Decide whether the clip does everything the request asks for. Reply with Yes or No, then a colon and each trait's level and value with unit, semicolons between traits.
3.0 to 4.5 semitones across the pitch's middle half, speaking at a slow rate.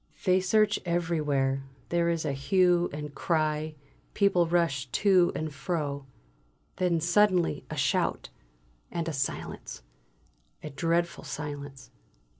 Yes: average, 3.5 semitones; slow, 115 wpm